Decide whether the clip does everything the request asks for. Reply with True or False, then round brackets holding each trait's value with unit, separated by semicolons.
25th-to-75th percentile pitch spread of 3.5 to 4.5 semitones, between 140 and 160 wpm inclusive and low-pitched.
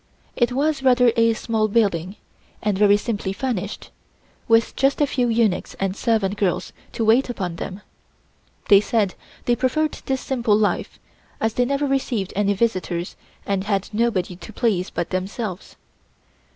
False (3.8 semitones; 150 wpm; 220 Hz)